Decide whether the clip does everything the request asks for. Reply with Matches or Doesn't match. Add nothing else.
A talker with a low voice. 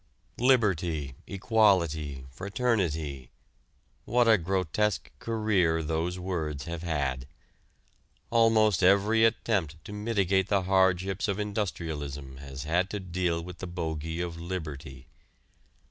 Matches